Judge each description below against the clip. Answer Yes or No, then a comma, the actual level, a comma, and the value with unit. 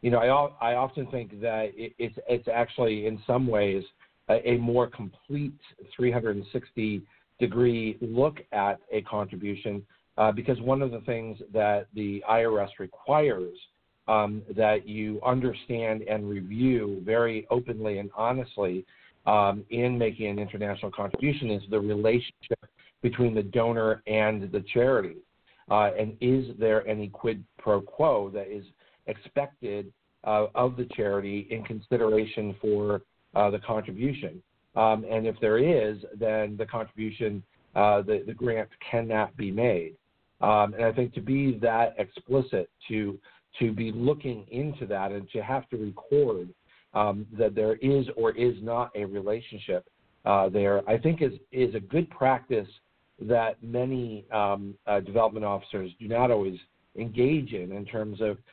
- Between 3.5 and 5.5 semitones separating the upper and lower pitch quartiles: No, average, 2.9 semitones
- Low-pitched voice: Yes, low, 110 Hz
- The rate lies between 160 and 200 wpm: No, average, 150 wpm